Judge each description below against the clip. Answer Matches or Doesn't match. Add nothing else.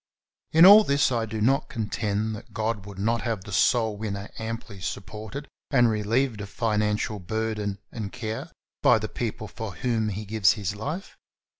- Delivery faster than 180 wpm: Doesn't match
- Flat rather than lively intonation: Matches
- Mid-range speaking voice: Doesn't match